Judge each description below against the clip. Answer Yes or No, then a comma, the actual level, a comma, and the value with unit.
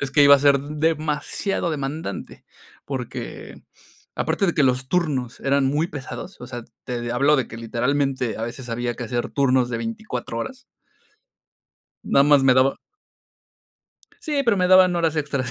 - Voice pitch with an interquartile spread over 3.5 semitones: Yes, average, 4.0 semitones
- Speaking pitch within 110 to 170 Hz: Yes, medium, 140 Hz